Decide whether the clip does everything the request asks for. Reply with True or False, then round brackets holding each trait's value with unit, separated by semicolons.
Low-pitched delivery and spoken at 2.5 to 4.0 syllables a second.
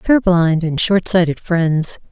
False (175 Hz; 3.6 syllables/s)